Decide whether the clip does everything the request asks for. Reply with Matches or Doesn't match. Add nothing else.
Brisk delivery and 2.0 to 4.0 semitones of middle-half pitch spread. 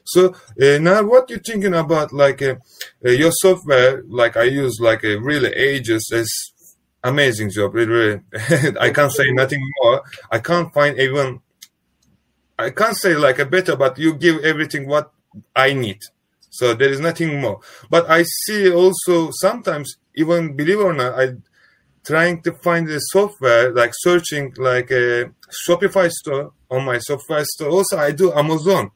Doesn't match